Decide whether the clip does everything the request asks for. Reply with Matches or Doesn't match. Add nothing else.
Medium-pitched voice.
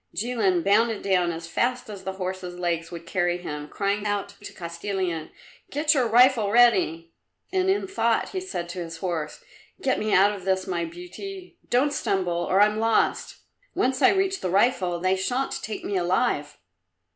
Doesn't match